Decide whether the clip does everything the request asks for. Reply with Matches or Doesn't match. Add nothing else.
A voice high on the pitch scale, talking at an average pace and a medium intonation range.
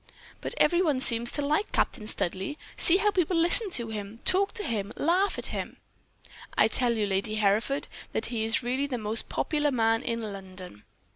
Doesn't match